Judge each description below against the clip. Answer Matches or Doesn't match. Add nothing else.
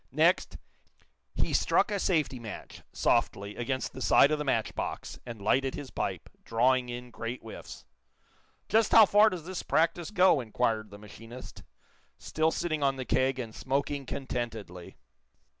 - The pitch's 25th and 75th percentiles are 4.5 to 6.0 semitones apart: Matches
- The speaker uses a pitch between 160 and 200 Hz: Doesn't match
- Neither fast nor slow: Matches